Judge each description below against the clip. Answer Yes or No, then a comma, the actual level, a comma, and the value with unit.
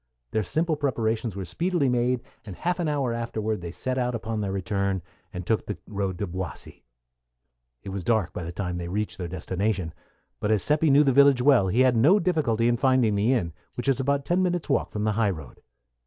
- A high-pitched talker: No, low, 115 Hz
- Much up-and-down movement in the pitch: Yes, wide, 5.7 semitones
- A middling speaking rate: No, fast, 215 wpm